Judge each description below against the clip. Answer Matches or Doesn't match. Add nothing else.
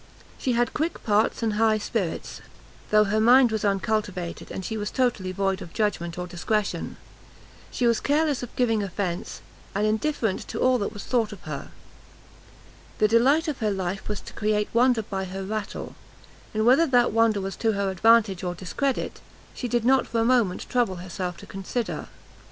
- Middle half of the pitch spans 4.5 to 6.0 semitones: Doesn't match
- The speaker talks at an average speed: Matches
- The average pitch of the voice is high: Matches